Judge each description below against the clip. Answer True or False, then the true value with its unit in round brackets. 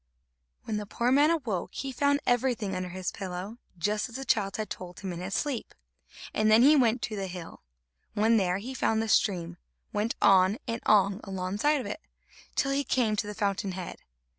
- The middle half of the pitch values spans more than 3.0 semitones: True (4.3 semitones)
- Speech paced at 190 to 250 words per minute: True (200 wpm)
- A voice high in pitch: True (210 Hz)